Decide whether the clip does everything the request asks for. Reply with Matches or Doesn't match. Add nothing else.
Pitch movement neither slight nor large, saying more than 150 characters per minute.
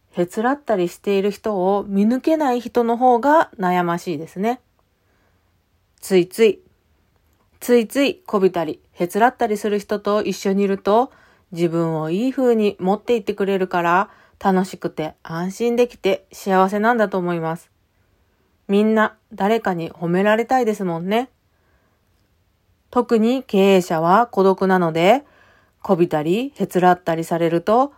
Matches